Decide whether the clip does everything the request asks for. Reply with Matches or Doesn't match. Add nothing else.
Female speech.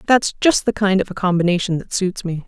Matches